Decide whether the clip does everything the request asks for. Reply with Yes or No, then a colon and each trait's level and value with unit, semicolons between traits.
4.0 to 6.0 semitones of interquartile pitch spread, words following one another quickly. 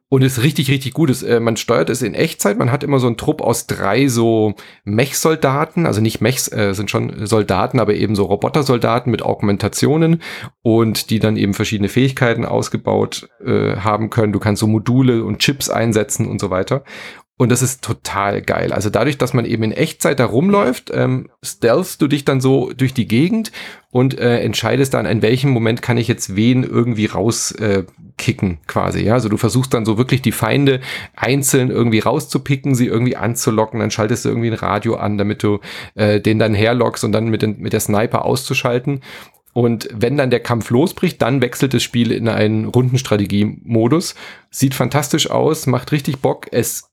No: average, 3.6 semitones; fast, 195 wpm